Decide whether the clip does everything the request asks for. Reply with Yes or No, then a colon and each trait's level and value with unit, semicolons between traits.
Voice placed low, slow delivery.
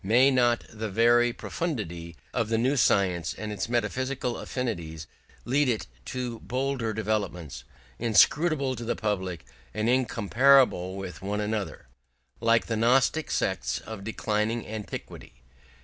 Yes: low, 115 Hz; slow, 130 wpm